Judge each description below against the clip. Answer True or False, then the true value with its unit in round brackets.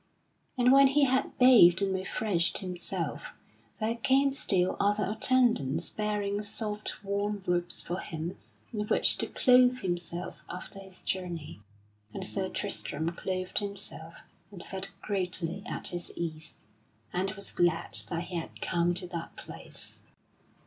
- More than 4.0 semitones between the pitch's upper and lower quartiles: False (3.4 semitones)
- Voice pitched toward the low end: False (190 Hz)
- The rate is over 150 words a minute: False (140 wpm)